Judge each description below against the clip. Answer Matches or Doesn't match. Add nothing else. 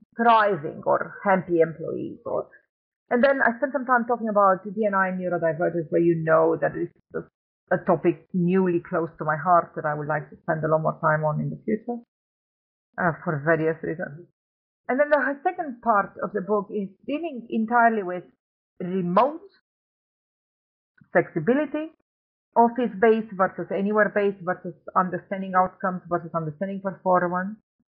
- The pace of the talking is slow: Doesn't match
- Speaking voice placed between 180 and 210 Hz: Matches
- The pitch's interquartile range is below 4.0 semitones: Doesn't match